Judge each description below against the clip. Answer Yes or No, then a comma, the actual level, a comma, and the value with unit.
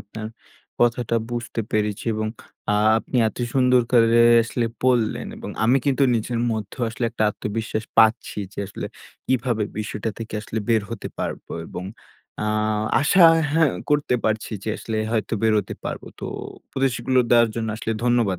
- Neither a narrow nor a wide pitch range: No, narrow, 2.2 semitones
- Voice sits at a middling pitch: No, low, 115 Hz